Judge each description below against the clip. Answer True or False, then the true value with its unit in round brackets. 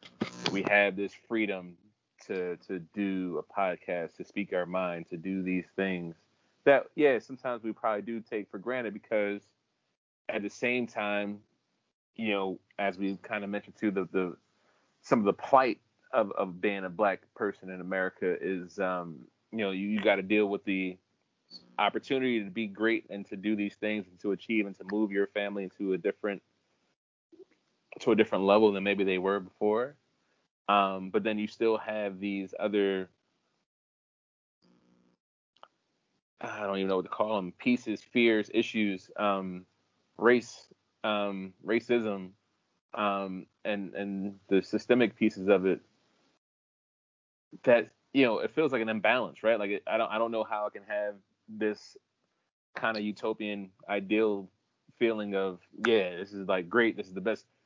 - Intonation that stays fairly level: True (2.2 semitones)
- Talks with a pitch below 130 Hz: True (100 Hz)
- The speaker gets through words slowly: False (165 wpm)